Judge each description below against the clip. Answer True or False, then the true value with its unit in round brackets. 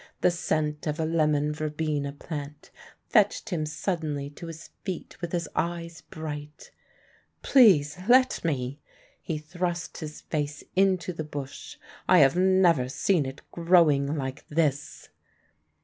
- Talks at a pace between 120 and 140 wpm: True (135 wpm)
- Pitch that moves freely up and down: False (2.8 semitones)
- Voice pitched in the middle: True (155 Hz)